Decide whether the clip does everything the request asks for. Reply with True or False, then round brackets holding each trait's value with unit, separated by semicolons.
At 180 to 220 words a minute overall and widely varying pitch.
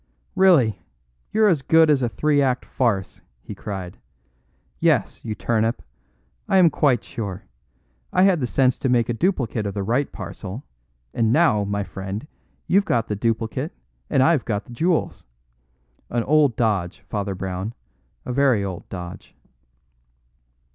False (150 wpm; 5.9 semitones)